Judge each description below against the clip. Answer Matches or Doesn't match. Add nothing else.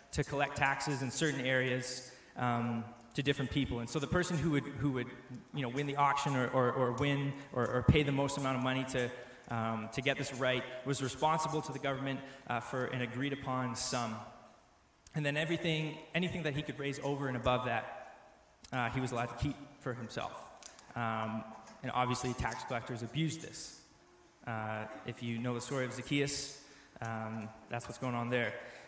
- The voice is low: Matches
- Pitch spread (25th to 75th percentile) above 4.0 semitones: Doesn't match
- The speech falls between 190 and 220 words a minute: Matches